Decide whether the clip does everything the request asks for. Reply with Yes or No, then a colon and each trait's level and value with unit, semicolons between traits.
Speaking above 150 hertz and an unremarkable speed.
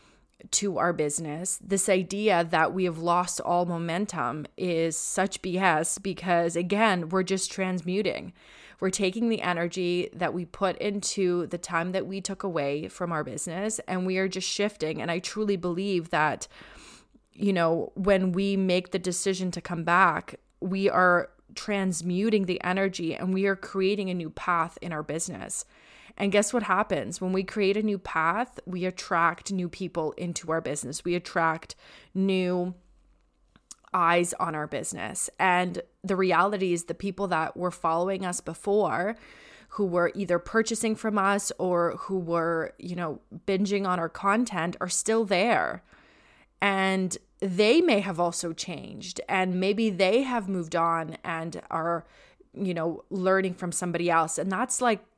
Yes: medium, 185 Hz; average, 160 wpm